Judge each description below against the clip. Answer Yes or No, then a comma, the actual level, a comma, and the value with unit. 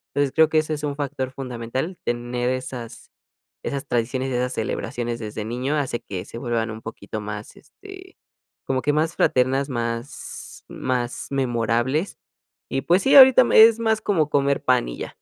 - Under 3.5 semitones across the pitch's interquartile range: No, average, 4.1 semitones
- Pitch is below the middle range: Yes, low, 130 Hz